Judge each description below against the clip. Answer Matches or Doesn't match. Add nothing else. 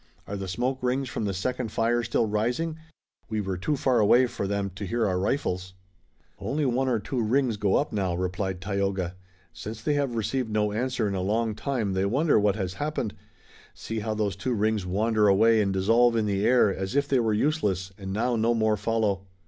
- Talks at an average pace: Doesn't match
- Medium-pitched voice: Doesn't match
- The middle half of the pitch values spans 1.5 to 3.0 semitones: Doesn't match